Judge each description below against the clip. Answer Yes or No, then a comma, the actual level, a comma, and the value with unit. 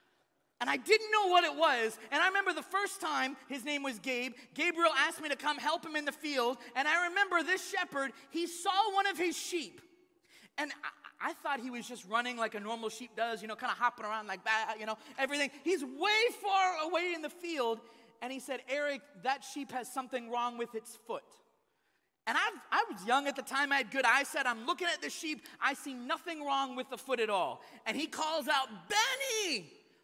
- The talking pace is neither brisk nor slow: No, fast, 225 wpm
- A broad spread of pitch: Yes, wide, 6.1 semitones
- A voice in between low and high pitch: No, very high, 280 Hz